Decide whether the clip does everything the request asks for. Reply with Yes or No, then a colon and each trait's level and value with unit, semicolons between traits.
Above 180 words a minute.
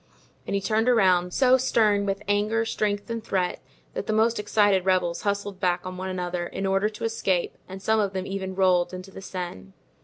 Yes: fast, 205 wpm